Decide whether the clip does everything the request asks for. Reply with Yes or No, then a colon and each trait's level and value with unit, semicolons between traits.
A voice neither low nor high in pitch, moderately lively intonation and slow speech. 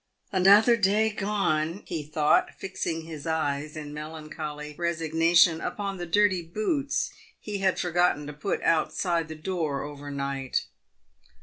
Yes: medium, 165 Hz; average, 4.1 semitones; slow, 125 wpm